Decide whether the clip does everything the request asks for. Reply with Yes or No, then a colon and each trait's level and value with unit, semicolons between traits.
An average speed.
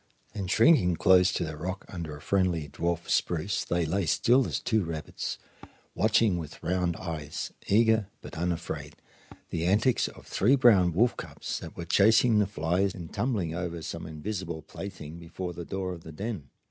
Yes: average, 170 wpm